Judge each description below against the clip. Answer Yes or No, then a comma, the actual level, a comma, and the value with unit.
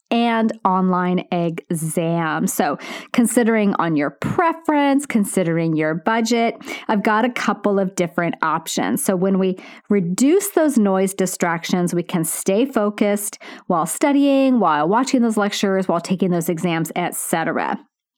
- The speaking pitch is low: No, high, 200 Hz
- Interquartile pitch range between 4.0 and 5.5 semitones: Yes, average, 4.9 semitones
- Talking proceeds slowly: Yes, slow, 130 wpm